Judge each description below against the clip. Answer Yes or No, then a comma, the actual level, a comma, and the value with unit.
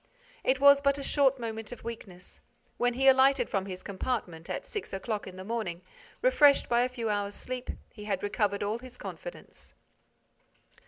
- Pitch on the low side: No, high, 235 Hz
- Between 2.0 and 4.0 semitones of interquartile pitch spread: No, average, 4.7 semitones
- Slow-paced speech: No, average, 175 wpm